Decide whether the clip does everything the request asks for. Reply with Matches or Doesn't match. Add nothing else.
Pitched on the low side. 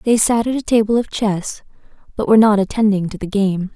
Doesn't match